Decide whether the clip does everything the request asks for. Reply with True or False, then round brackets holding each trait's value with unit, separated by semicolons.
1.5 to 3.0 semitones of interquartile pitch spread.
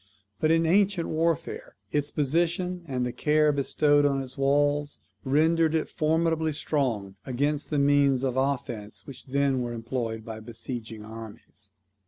False (4.1 semitones)